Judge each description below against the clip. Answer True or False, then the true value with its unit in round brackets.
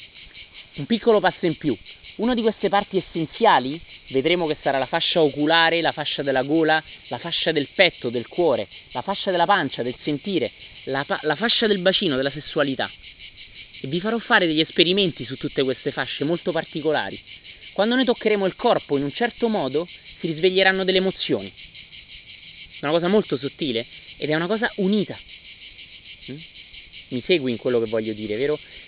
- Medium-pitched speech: True (155 Hz)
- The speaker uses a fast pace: True (175 wpm)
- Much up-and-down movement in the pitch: True (6.7 semitones)